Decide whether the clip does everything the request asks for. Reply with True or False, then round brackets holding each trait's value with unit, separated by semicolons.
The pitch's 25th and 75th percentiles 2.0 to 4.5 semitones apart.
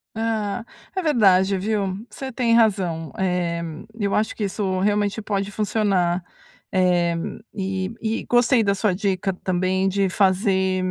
True (2.4 semitones)